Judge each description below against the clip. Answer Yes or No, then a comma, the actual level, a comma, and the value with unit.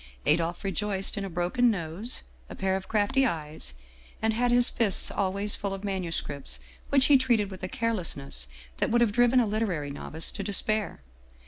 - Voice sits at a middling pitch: No, high, 200 Hz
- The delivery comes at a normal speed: Yes, average, 180 wpm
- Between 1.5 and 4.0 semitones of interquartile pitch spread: No, average, 4.7 semitones